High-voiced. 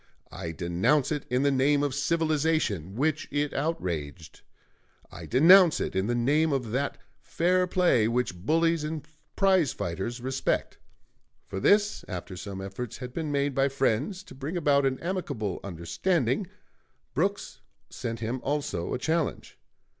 No: low, 135 Hz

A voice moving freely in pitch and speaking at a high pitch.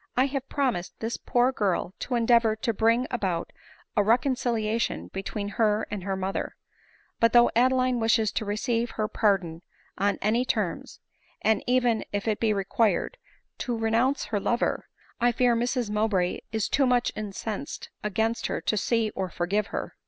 No: average, 2.8 semitones; high, 225 Hz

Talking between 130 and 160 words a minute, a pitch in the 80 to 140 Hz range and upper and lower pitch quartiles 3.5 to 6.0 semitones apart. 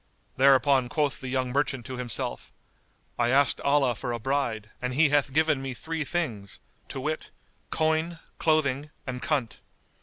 No: average, 155 wpm; low, 135 Hz; average, 3.1 semitones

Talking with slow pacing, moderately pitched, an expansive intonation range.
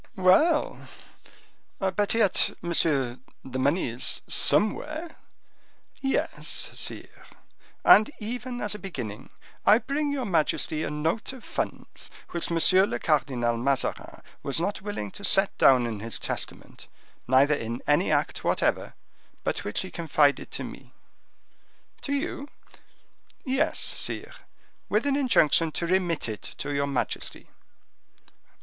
Yes: slow, 130 wpm; medium, 170 Hz; wide, 7.8 semitones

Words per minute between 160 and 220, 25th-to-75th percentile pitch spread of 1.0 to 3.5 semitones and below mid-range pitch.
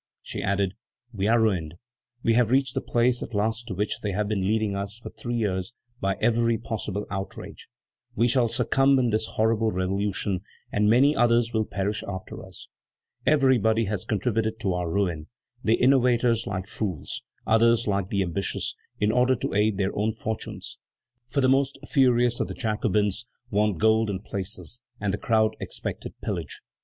Yes: average, 170 wpm; average, 3.0 semitones; low, 110 Hz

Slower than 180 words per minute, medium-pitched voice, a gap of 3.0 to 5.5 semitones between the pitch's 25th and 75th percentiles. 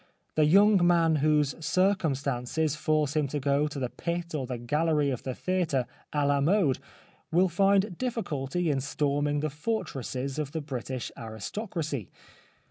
Yes: average, 150 wpm; medium, 150 Hz; average, 3.8 semitones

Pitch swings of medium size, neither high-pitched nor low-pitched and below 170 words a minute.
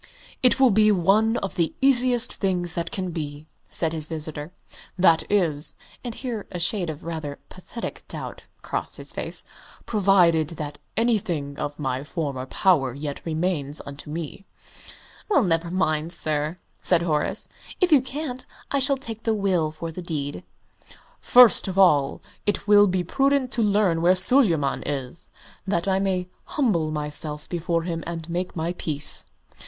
Yes: average, 5.0 semitones; medium, 175 Hz; average, 160 wpm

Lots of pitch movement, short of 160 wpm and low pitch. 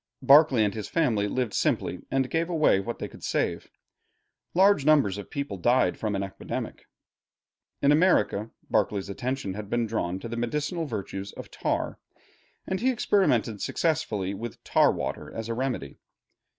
No: wide, 6.5 semitones; average, 165 wpm; low, 120 Hz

